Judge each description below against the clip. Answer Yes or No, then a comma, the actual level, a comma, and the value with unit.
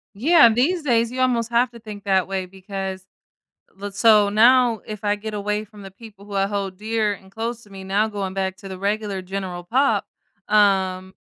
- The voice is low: No, high, 205 Hz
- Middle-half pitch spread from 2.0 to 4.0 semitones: Yes, average, 2.8 semitones